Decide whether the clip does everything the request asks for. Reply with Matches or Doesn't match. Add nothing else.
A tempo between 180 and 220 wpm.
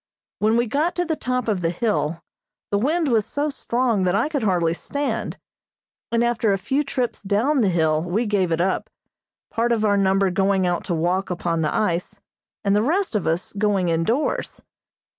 Matches